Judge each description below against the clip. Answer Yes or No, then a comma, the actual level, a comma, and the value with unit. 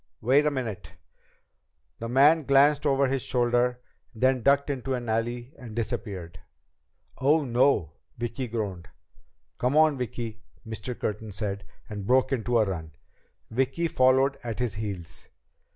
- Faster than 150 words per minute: No, average, 140 wpm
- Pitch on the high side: No, low, 120 Hz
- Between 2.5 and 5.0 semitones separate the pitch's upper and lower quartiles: Yes, average, 3.7 semitones